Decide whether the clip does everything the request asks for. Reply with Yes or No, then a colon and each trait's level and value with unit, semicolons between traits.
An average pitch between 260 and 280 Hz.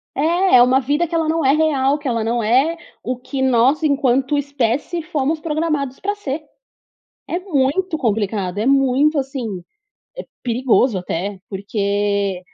Yes: very high, 270 Hz